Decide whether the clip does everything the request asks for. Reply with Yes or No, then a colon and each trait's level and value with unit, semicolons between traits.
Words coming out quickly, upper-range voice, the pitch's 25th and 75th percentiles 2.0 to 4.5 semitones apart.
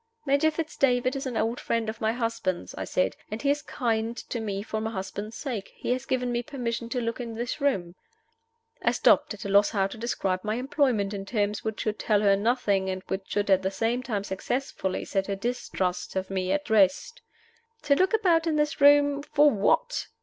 No: fast, 215 wpm; high, 230 Hz; wide, 5.5 semitones